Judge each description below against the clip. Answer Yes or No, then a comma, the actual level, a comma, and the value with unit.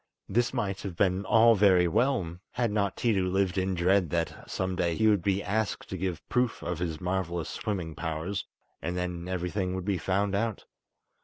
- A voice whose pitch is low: Yes, very low, 95 Hz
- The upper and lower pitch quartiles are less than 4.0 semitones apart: Yes, narrow, 2.6 semitones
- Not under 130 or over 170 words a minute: No, average, 185 wpm